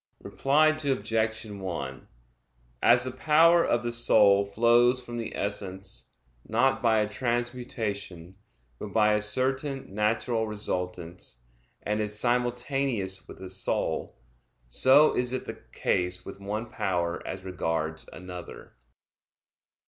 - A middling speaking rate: No, slow, 120 wpm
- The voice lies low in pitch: Yes, low, 110 Hz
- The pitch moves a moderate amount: Yes, average, 4.4 semitones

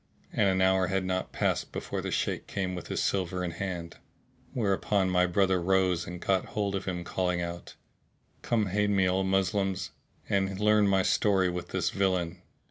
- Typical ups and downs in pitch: No, narrow, 1.5 semitones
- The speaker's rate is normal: Yes, average, 185 wpm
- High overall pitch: No, very low, 95 Hz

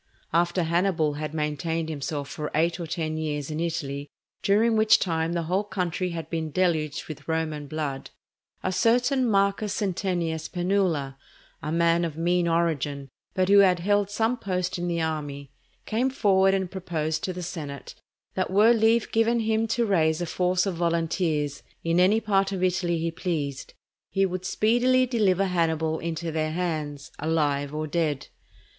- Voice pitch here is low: No, medium, 170 Hz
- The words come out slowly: No, average, 165 wpm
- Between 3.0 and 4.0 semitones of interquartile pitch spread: Yes, average, 3.6 semitones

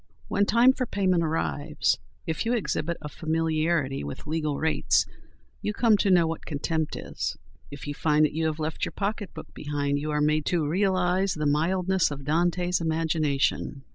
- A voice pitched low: No, medium, 160 Hz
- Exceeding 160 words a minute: Yes, average, 170 wpm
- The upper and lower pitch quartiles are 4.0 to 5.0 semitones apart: No, average, 3.3 semitones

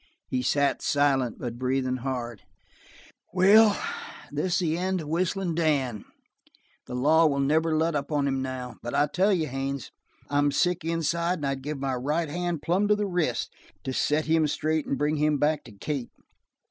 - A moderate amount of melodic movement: Yes, average, 3.8 semitones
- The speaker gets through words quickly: No, average, 185 wpm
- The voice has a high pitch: No, medium, 150 Hz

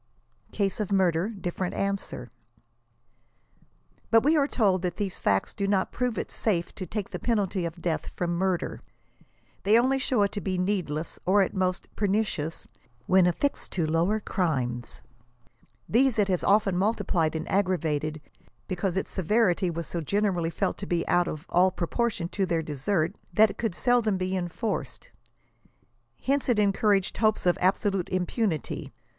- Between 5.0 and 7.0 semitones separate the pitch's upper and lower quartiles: No, average, 3.4 semitones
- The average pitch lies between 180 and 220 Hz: Yes, high, 190 Hz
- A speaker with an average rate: Yes, average, 160 wpm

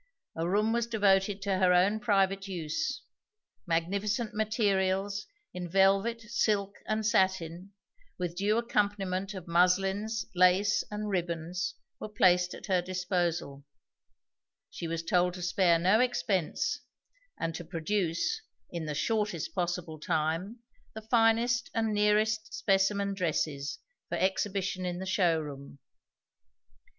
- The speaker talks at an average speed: No, slow, 125 wpm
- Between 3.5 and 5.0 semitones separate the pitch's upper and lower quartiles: No, average, 3.1 semitones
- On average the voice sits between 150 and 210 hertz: Yes, high, 190 Hz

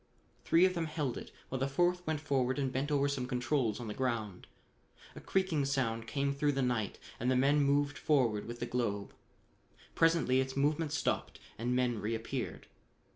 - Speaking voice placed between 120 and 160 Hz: Yes, low, 135 Hz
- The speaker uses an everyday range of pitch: Yes, average, 3.3 semitones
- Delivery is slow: No, average, 180 wpm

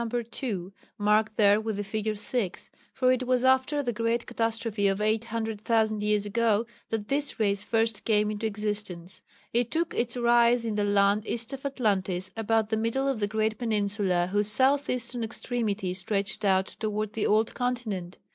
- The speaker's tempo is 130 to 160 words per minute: No, average, 170 wpm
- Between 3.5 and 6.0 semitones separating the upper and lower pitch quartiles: No, narrow, 2.4 semitones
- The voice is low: No, high, 220 Hz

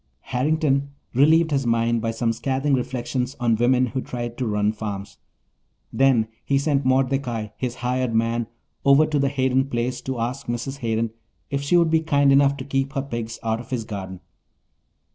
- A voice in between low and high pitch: No, low, 130 Hz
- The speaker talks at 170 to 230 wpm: Yes, average, 180 wpm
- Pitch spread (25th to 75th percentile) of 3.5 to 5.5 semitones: No, average, 3.0 semitones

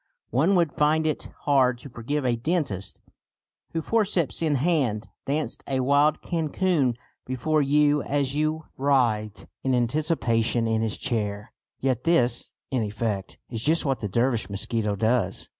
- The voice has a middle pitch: No, low, 130 Hz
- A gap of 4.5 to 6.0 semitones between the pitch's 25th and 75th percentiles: Yes, average, 4.9 semitones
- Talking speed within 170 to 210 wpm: No, average, 145 wpm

